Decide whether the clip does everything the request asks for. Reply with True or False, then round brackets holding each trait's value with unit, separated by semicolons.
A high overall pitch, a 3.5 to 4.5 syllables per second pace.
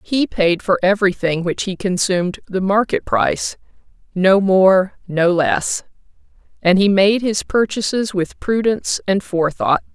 True (195 Hz; 4.4 syllables/s)